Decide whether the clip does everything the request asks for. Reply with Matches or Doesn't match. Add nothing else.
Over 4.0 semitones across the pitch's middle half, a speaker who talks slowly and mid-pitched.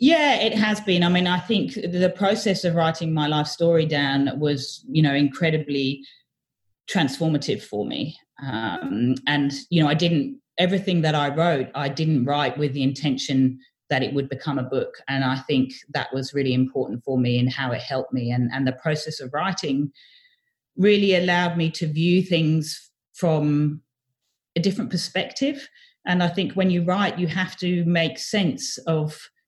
Doesn't match